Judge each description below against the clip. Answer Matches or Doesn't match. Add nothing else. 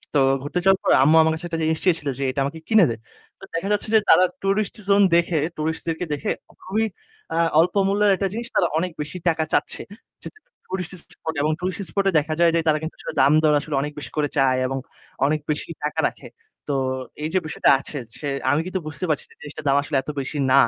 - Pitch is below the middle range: Doesn't match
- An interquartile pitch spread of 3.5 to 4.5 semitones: Matches